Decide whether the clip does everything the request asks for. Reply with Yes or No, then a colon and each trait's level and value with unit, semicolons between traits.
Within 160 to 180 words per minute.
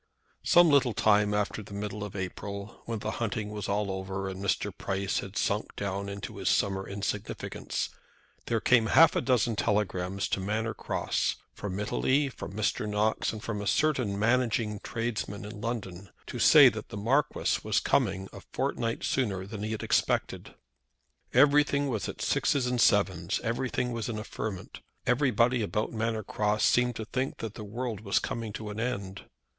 Yes: average, 175 wpm